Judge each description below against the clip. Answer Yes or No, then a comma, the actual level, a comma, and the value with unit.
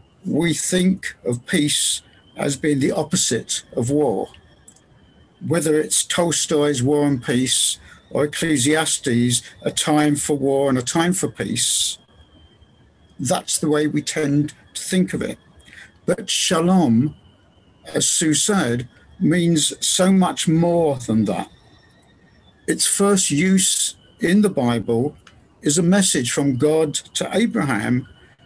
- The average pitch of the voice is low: No, medium, 150 Hz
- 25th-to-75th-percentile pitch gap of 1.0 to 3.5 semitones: No, average, 4.9 semitones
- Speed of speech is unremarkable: No, slow, 125 wpm